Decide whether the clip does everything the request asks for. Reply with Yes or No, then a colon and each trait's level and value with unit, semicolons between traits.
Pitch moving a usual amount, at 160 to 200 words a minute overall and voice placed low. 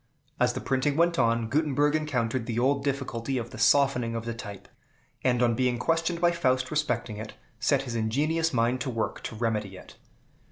Yes: average, 3.7 semitones; average, 190 wpm; low, 125 Hz